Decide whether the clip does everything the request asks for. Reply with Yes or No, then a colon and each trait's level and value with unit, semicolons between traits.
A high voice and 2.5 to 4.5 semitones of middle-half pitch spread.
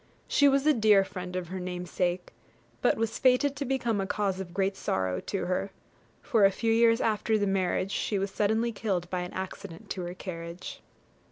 Yes: high, 195 Hz; average, 3.7 semitones